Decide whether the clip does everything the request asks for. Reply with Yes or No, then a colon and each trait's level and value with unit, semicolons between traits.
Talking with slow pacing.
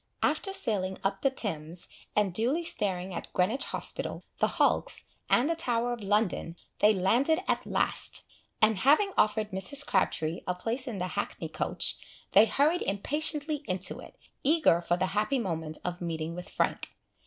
No: average, 165 wpm